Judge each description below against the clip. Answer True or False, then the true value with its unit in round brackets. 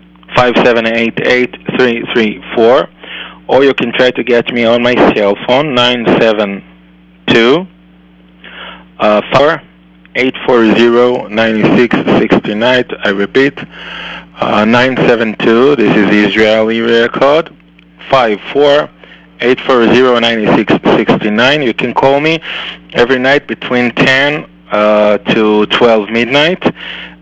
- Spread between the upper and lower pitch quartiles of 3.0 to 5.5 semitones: True (3.9 semitones)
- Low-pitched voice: True (115 Hz)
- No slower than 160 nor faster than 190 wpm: False (140 wpm)